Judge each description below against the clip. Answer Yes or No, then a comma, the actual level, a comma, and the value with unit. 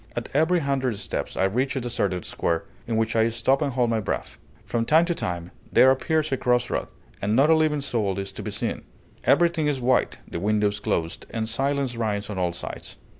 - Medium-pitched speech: No, low, 120 Hz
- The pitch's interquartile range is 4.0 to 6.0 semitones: Yes, average, 5.1 semitones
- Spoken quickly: Yes, fast, 215 wpm